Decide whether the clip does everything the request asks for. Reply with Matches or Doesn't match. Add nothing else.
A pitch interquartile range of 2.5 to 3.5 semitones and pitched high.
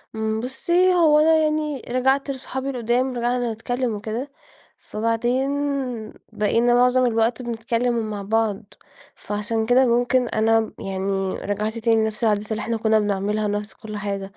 Matches